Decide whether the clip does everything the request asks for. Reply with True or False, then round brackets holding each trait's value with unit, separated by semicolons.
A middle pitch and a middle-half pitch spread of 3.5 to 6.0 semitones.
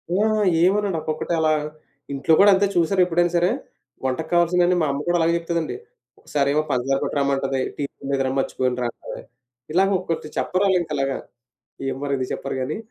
True (155 Hz; 4.2 semitones)